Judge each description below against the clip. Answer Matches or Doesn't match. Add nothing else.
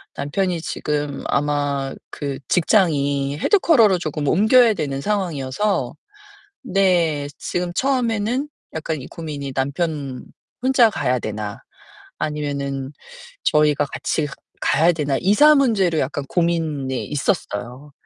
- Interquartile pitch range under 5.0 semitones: Doesn't match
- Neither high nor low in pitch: Matches